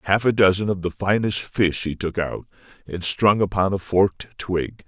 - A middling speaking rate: Yes, average, 195 wpm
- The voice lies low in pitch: Yes, very low, 95 Hz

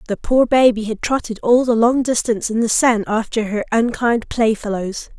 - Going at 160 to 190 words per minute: Yes, average, 185 wpm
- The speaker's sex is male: No, female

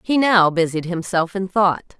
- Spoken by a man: No, female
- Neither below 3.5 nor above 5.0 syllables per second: Yes, 4.2 syllables/s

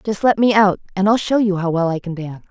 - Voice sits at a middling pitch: No, high, 195 Hz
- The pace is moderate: No, fast, 310 wpm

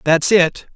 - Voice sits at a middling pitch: Yes, medium, 175 Hz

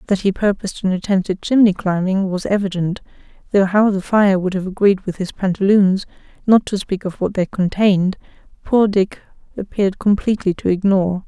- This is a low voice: No, high, 195 Hz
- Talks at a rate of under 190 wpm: Yes, average, 175 wpm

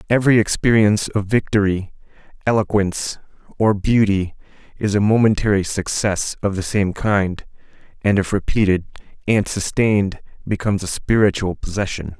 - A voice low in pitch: Yes, low, 100 Hz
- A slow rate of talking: Yes, slow, 120 wpm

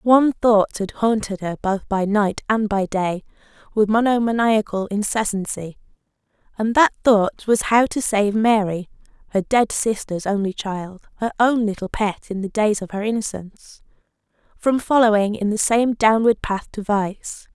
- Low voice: No, high, 210 Hz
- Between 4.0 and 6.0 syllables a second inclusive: No, 3.8 syllables/s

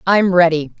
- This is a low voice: No, medium, 175 Hz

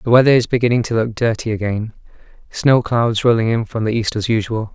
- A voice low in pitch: Yes, low, 115 Hz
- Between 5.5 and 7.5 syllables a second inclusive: Yes, 5.9 syllables/s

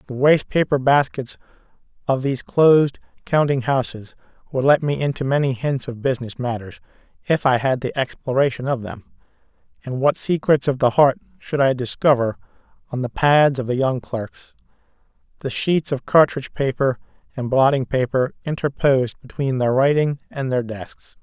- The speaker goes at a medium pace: Yes, average, 155 wpm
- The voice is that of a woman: No, male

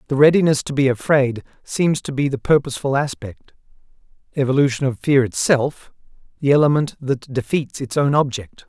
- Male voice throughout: Yes, male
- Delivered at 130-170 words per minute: Yes, average, 150 wpm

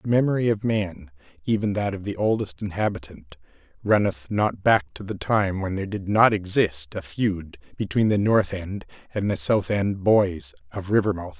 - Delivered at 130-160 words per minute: No, average, 180 wpm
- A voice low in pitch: Yes, low, 105 Hz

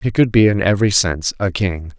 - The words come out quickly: Yes, fast, 240 wpm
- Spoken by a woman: No, male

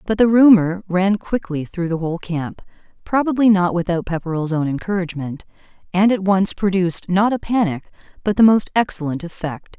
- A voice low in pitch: No, medium, 185 Hz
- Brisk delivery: No, average, 165 wpm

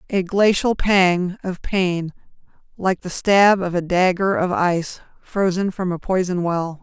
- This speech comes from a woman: Yes, female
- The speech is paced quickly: No, average, 160 wpm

